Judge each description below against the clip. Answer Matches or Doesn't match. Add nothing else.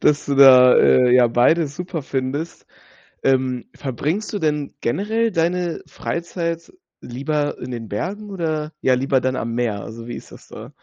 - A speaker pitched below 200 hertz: Matches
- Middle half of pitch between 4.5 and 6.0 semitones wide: Matches